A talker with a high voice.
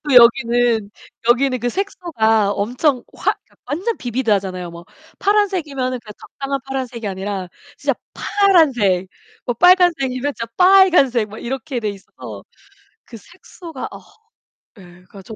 Yes: high, 245 Hz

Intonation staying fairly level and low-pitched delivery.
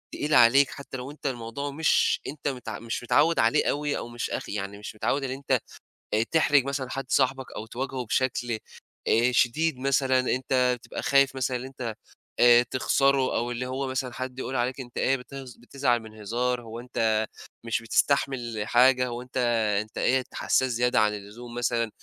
Yes: narrow, 2.1 semitones; low, 125 Hz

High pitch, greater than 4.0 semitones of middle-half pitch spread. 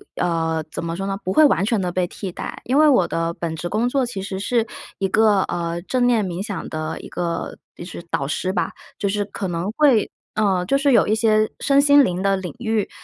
Yes: high, 195 Hz; average, 4.5 semitones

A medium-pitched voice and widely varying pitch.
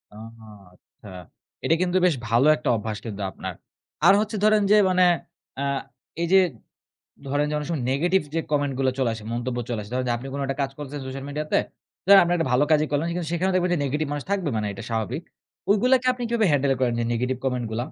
Yes: medium, 145 Hz; wide, 6.4 semitones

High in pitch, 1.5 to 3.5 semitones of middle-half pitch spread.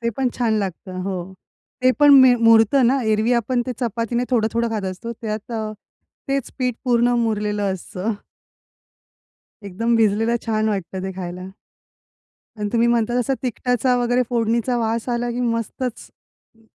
Yes: high, 230 Hz; narrow, 2.4 semitones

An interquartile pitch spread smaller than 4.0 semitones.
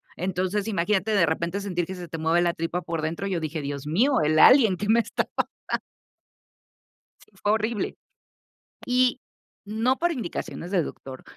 No: average, 4.7 semitones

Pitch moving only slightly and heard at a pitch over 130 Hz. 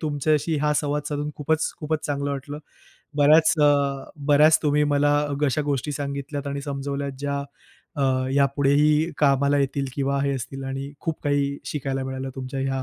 Yes: narrow, 1.2 semitones; medium, 140 Hz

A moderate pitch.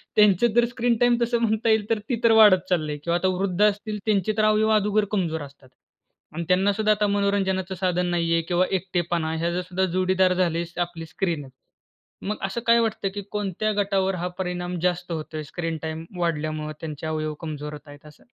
Yes: medium, 180 Hz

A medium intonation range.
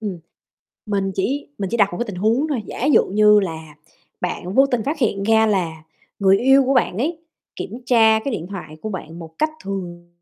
Yes: average, 5.0 semitones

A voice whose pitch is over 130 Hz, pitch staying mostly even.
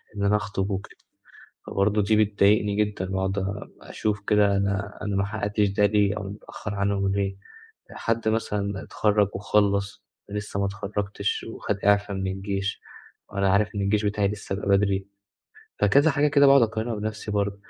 No: low, 100 Hz; narrow, 1.1 semitones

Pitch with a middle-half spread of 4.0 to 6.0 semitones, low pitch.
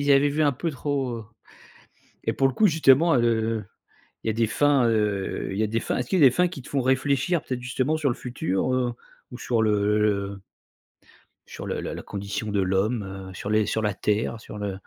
Yes: average, 4.5 semitones; low, 120 Hz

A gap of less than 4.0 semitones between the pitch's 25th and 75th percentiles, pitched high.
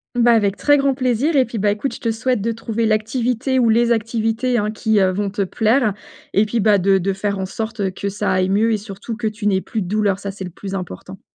Yes: average, 2.9 semitones; high, 215 Hz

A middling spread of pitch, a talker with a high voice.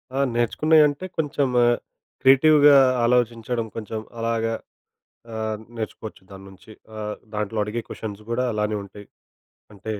No: average, 3.5 semitones; low, 115 Hz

